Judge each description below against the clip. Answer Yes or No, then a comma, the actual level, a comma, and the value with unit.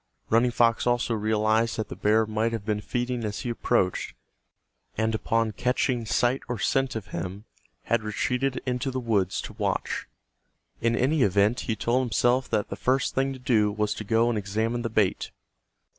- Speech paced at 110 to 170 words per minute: No, average, 180 wpm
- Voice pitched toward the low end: Yes, low, 115 Hz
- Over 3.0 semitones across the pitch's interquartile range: No, narrow, 2.4 semitones